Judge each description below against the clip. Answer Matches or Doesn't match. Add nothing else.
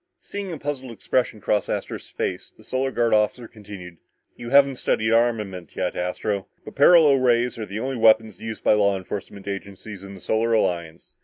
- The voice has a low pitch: Matches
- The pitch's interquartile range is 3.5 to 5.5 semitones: Matches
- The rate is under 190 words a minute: Matches